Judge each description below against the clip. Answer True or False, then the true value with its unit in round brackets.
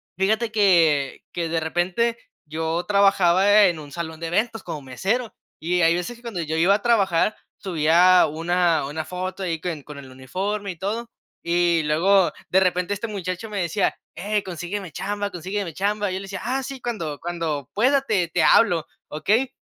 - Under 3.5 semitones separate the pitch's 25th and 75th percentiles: False (3.8 semitones)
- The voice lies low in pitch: False (180 Hz)